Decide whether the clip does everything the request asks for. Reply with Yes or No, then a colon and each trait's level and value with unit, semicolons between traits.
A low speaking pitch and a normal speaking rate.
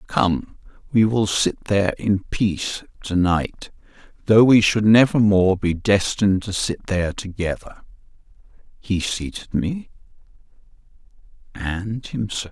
No: low, 100 Hz; slow, 120 wpm